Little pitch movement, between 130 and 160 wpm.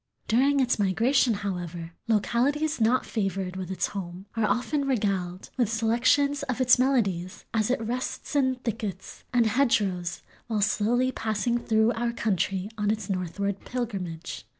No: average, 4.4 semitones; average, 145 wpm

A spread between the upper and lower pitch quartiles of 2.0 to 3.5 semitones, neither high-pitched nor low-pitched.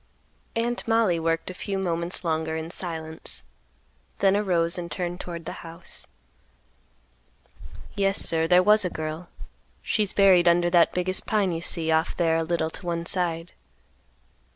Yes: narrow, 2.4 semitones; medium, 175 Hz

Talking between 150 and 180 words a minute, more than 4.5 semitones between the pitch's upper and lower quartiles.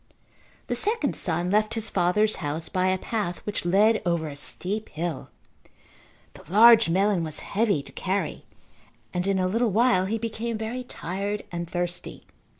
No: average, 160 wpm; average, 3.9 semitones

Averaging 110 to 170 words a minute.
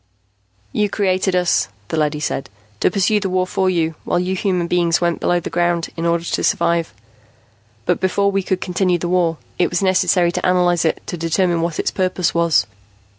No: average, 195 wpm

